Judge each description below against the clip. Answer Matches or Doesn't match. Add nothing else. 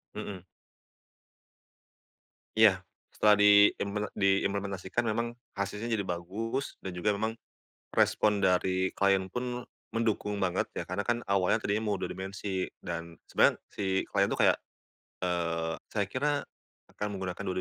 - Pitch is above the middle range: Doesn't match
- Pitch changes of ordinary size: Doesn't match